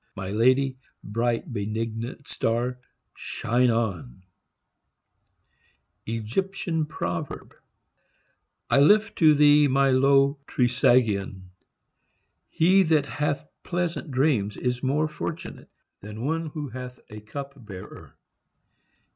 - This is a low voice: Yes, low, 130 Hz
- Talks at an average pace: No, slow, 90 wpm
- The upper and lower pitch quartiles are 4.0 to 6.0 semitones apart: Yes, average, 4.8 semitones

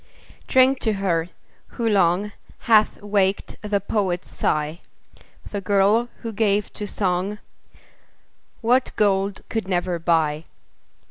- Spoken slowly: Yes, slow, 115 wpm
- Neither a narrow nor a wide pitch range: Yes, average, 3.0 semitones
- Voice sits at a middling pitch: No, high, 200 Hz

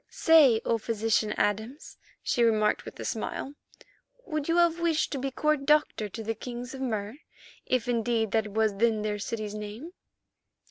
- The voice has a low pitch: No, high, 230 Hz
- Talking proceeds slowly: No, average, 170 wpm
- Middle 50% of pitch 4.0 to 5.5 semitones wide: Yes, average, 4.4 semitones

